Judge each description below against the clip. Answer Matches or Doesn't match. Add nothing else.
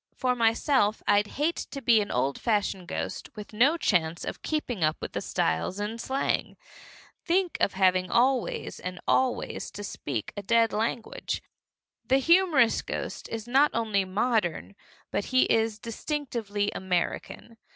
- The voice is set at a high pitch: Matches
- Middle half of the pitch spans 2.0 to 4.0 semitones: Doesn't match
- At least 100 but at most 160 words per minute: Matches